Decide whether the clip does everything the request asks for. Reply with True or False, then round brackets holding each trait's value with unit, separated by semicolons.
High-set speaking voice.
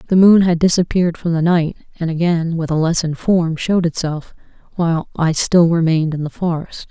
False (165 Hz)